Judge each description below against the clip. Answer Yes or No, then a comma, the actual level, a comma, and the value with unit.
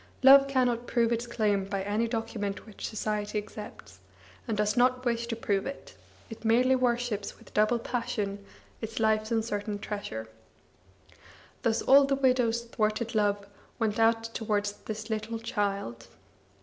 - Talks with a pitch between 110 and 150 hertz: No, high, 225 Hz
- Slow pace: No, average, 150 wpm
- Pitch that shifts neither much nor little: No, narrow, 2.3 semitones